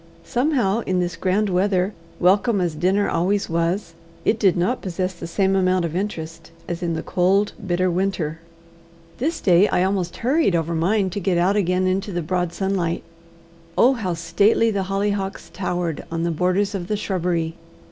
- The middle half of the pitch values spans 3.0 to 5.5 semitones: No, narrow, 2.6 semitones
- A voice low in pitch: No, medium, 185 Hz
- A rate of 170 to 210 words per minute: Yes, average, 175 wpm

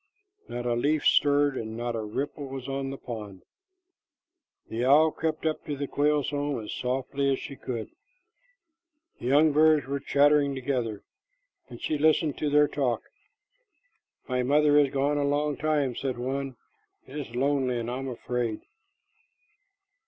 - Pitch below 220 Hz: Yes, medium, 140 Hz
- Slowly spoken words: No, average, 160 wpm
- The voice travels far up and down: No, average, 2.8 semitones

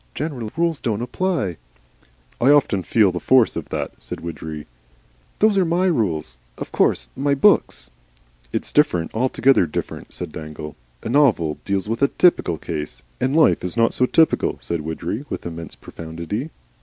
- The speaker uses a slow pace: No, average, 160 wpm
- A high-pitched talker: No, low, 105 Hz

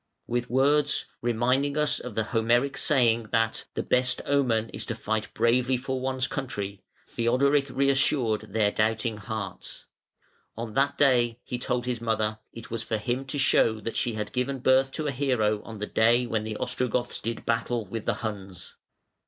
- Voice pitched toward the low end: Yes, low, 120 Hz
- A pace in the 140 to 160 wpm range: No, average, 175 wpm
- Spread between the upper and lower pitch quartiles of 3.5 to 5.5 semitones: No, average, 2.9 semitones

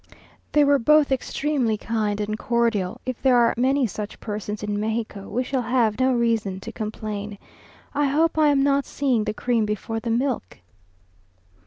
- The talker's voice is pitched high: Yes, high, 235 Hz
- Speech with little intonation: No, average, 4.0 semitones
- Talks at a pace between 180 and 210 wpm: No, average, 170 wpm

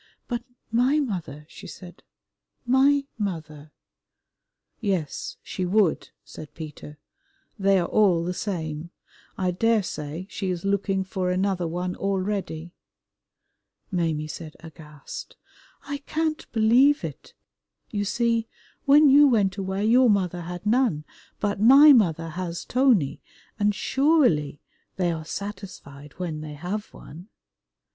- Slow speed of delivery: Yes, slow, 120 wpm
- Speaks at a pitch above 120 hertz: Yes, high, 190 Hz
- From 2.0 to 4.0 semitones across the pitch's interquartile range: No, wide, 5.5 semitones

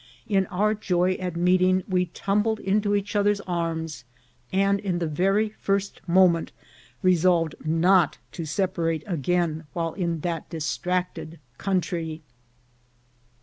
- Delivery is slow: Yes, slow, 120 wpm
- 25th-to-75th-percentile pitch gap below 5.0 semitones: Yes, average, 2.9 semitones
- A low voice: No, medium, 180 Hz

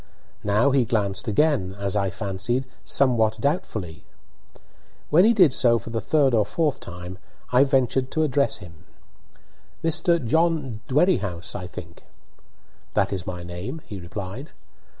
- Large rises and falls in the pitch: Yes, wide, 6.6 semitones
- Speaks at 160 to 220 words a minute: No, average, 140 wpm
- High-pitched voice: No, low, 115 Hz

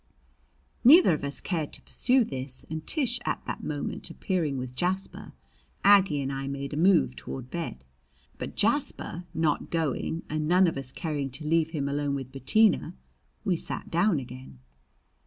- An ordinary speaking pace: Yes, average, 165 wpm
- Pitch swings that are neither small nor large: Yes, average, 4.5 semitones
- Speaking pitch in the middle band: Yes, medium, 155 Hz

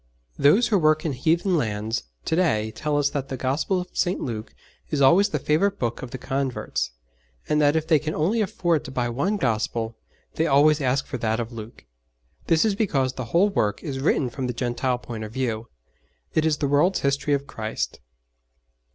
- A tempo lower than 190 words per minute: No, average, 200 wpm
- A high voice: No, medium, 140 Hz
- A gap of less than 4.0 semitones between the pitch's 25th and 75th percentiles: No, average, 5.0 semitones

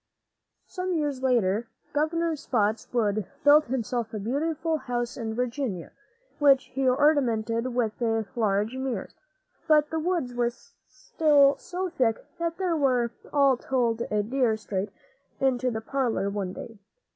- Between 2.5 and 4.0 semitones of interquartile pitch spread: No, average, 4.6 semitones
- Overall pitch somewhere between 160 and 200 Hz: No, very high, 250 Hz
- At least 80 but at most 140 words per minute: Yes, slow, 135 wpm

